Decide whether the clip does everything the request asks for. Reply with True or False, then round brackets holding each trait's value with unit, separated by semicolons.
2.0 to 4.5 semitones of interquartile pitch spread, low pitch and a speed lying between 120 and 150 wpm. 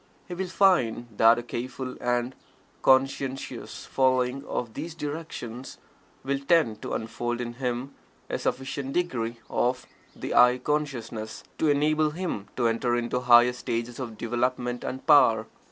True (2.7 semitones; 125 Hz; 140 wpm)